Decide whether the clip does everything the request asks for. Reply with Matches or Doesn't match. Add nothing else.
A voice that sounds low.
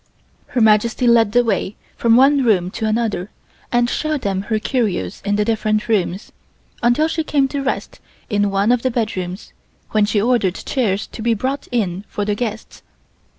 Doesn't match